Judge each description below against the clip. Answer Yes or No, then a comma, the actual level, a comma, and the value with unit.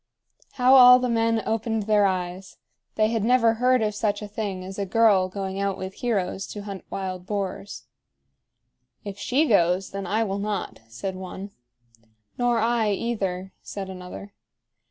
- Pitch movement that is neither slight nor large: Yes, average, 3.0 semitones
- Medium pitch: No, high, 205 Hz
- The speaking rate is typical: Yes, average, 160 wpm